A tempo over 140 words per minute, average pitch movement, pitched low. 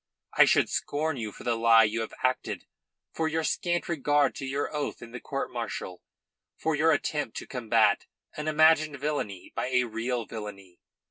Yes: average, 180 wpm; average, 4.9 semitones; low, 130 Hz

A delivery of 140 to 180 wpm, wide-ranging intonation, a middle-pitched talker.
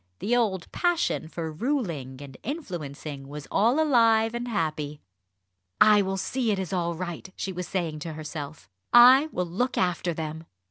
Yes: average, 165 wpm; wide, 6.9 semitones; medium, 180 Hz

